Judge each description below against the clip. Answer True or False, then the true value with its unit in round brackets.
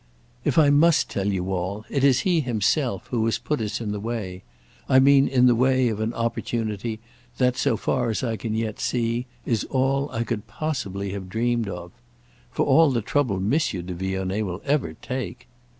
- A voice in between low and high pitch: False (115 Hz)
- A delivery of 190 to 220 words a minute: True (195 wpm)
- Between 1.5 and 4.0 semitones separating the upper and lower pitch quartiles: False (4.5 semitones)